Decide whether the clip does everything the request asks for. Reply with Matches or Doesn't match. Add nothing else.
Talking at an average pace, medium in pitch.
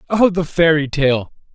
Matches